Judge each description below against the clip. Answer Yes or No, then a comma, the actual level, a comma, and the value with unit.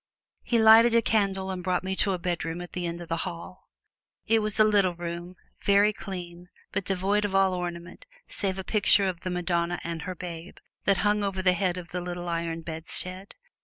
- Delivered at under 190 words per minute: No, fast, 205 wpm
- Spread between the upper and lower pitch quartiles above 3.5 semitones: No, narrow, 2.5 semitones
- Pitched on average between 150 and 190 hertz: Yes, medium, 185 Hz